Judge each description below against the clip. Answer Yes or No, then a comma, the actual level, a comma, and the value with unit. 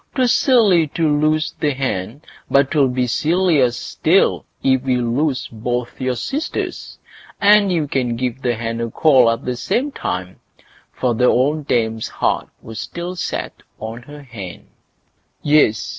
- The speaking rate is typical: Yes, average, 150 wpm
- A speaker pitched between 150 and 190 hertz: No, low, 130 Hz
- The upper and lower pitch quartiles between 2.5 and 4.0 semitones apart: No, average, 4.9 semitones